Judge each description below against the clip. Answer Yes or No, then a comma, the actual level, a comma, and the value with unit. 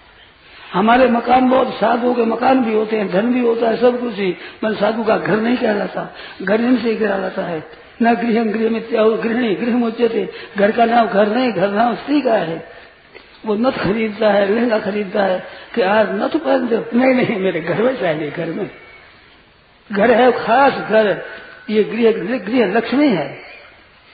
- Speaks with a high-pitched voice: Yes, high, 225 Hz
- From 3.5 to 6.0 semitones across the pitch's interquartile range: No, average, 2.9 semitones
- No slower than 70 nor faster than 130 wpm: No, average, 175 wpm